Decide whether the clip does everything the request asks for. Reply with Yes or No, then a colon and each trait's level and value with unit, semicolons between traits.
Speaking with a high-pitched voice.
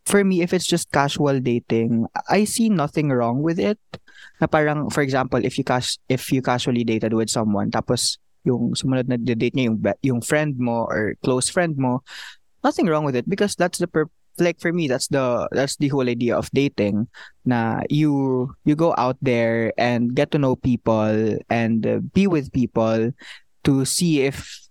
No: low, 130 Hz